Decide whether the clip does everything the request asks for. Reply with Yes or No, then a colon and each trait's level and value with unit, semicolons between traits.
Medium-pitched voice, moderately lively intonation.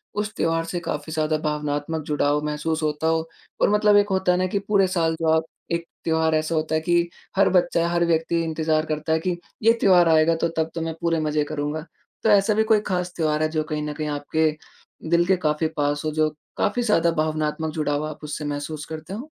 No: medium, 160 Hz; narrow, 2.0 semitones